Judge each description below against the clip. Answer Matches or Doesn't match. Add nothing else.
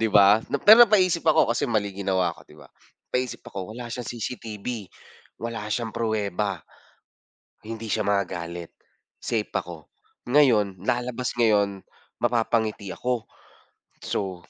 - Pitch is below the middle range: Matches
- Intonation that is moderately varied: Matches